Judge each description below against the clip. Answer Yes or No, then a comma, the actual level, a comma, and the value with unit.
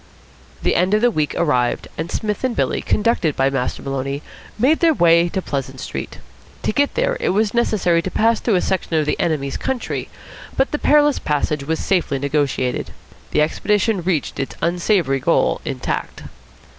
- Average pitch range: No, wide, 7.3 semitones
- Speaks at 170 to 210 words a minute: Yes, average, 175 wpm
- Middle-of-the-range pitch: Yes, medium, 175 Hz